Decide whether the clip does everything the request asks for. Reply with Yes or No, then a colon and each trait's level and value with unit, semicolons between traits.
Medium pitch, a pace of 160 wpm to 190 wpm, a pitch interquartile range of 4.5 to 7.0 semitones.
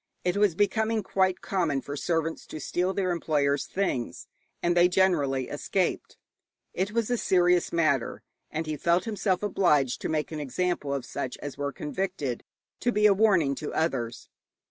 Yes: medium, 175 Hz; average, 165 wpm; average, 4.9 semitones